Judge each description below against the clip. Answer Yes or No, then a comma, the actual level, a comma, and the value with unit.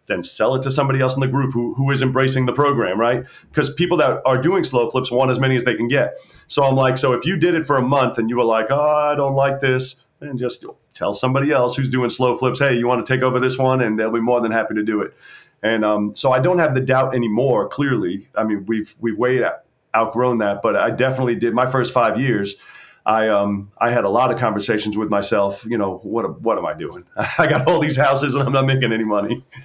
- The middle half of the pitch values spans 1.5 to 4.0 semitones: Yes, average, 2.7 semitones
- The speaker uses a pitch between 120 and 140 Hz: Yes, low, 125 Hz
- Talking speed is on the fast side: Yes, fast, 260 wpm